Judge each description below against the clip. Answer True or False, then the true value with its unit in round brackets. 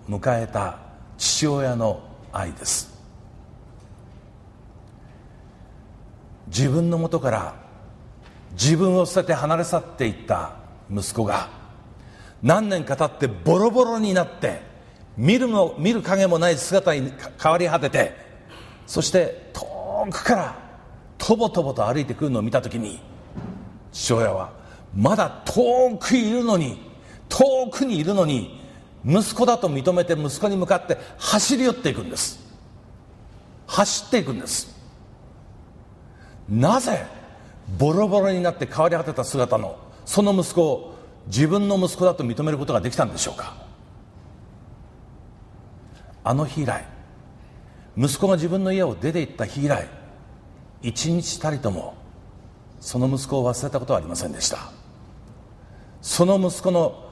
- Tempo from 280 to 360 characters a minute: False (245 characters per minute)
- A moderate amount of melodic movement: False (8.2 semitones)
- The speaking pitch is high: False (140 Hz)